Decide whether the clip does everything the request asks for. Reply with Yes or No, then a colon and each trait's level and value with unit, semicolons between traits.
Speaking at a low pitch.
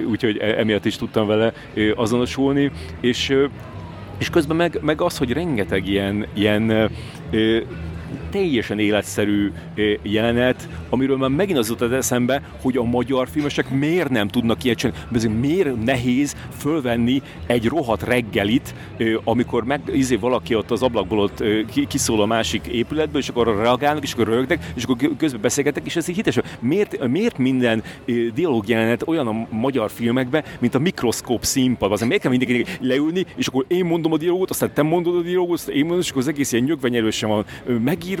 Yes: low, 125 Hz